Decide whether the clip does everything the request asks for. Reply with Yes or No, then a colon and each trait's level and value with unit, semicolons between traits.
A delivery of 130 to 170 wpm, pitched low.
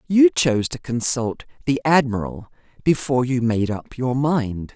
Yes: average, 150 wpm; low, 125 Hz